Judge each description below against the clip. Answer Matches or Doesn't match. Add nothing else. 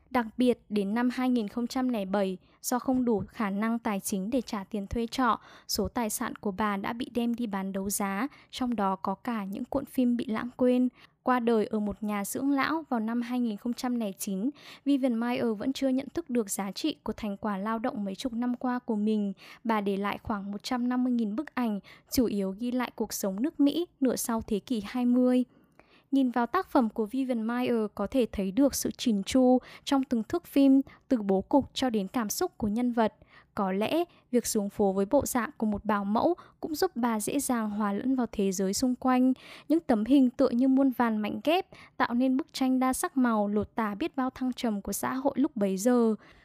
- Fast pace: Doesn't match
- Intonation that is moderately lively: Matches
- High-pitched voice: Matches